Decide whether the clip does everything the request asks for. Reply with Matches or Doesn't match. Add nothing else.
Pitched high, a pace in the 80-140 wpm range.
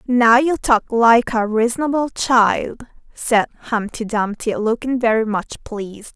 Matches